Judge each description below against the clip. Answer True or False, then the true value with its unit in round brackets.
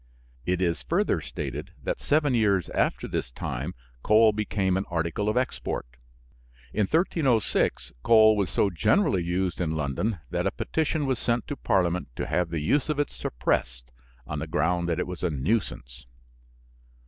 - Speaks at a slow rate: False (165 wpm)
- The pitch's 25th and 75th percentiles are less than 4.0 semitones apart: False (5.6 semitones)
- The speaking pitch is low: True (95 Hz)